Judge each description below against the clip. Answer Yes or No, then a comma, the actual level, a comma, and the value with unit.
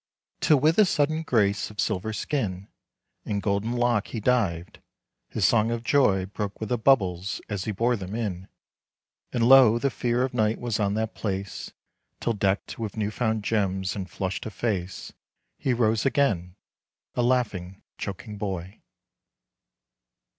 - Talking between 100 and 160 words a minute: Yes, average, 155 wpm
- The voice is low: Yes, low, 110 Hz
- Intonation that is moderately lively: Yes, average, 3.6 semitones